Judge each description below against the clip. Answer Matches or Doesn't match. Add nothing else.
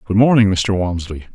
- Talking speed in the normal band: Matches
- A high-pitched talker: Doesn't match